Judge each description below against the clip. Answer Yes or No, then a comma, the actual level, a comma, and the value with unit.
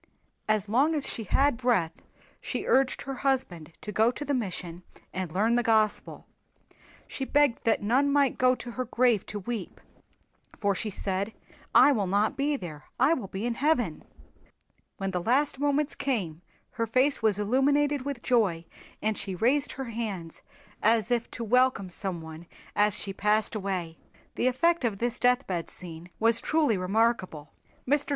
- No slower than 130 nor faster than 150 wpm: No, average, 165 wpm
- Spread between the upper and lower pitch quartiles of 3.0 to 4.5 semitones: No, average, 5.1 semitones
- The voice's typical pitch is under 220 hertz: No, high, 225 Hz